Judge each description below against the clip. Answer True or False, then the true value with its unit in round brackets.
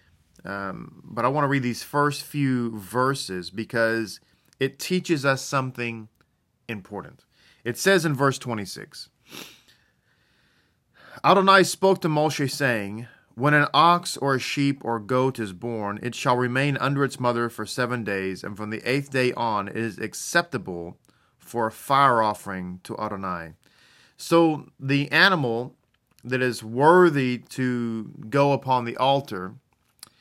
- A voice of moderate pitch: False (125 Hz)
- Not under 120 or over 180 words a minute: True (140 wpm)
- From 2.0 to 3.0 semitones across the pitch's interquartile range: False (4.2 semitones)